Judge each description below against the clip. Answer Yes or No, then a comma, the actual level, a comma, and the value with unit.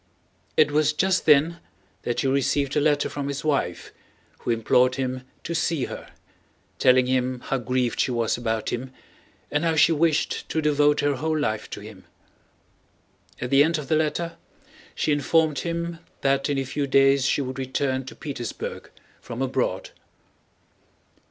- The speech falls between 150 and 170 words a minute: Yes, average, 165 wpm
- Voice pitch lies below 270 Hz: Yes, medium, 140 Hz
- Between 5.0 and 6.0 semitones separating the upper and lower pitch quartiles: No, average, 3.0 semitones